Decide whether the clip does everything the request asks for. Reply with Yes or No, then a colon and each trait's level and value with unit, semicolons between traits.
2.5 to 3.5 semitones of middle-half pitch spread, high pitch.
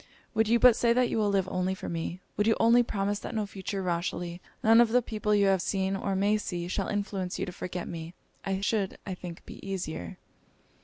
Yes: average, 2.9 semitones; high, 195 Hz